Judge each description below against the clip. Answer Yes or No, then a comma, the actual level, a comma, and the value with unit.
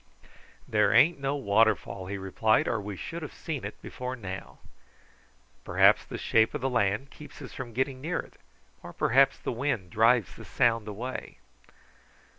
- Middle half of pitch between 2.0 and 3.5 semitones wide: No, average, 4.7 semitones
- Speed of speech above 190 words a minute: No, average, 165 wpm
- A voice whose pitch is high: No, low, 120 Hz